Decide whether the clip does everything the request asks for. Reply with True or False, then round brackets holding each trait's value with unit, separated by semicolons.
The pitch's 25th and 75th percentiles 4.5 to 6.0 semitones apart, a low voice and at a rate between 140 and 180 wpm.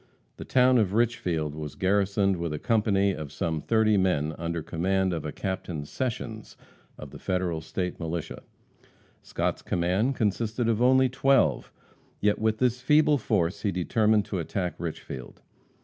True (4.9 semitones; 95 Hz; 150 wpm)